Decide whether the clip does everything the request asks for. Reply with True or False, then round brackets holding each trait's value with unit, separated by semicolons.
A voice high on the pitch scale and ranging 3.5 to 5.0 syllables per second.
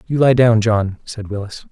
False (110 Hz; 4.6 syllables/s)